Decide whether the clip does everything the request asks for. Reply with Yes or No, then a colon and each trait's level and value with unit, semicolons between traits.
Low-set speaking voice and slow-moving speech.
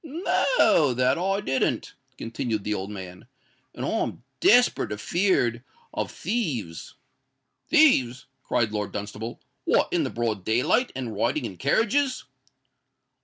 Yes: low, 125 Hz; slow, 120 wpm